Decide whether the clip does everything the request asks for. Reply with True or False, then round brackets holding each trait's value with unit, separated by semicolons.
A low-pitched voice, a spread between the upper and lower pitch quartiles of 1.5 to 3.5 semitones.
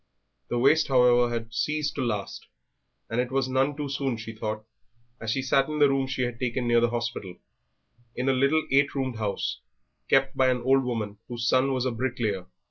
True (125 Hz; 2.5 semitones)